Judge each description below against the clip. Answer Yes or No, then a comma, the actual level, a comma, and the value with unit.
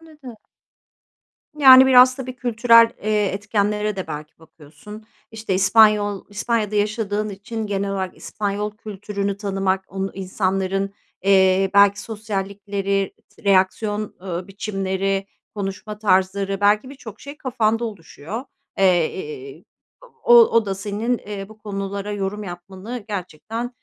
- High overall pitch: Yes, high, 205 Hz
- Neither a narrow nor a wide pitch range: No, narrow, 2.2 semitones